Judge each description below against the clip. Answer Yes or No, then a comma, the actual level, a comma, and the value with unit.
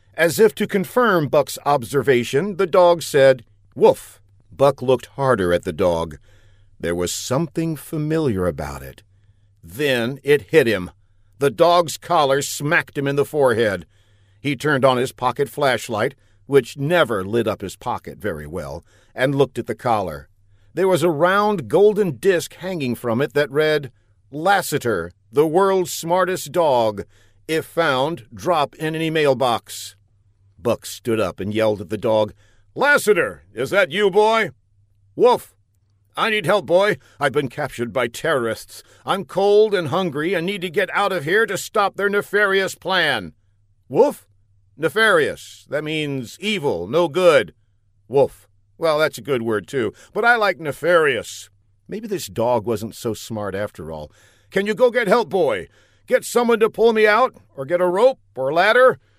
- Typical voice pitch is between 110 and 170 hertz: Yes, low, 135 Hz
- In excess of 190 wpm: No, average, 160 wpm